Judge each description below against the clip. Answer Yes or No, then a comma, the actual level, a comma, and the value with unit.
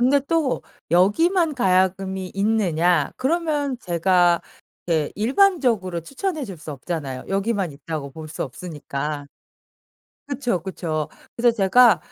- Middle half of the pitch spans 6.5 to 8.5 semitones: Yes, wide, 7.4 semitones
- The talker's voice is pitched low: No, high, 190 Hz